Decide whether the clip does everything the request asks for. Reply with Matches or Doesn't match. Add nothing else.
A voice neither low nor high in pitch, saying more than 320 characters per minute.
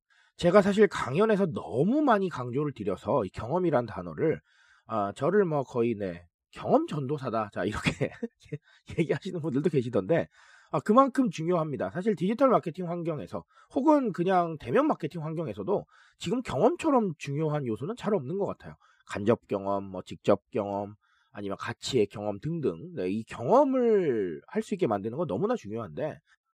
Matches